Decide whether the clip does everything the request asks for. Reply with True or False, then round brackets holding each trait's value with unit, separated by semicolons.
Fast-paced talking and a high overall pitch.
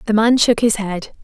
True (240 wpm; 220 Hz)